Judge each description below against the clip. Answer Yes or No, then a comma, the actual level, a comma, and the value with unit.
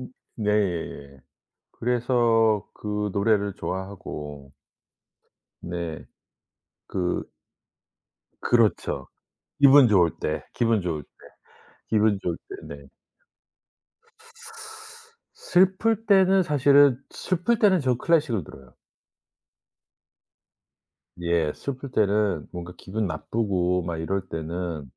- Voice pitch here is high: No, low, 105 Hz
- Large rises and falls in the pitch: Yes, wide, 6.9 semitones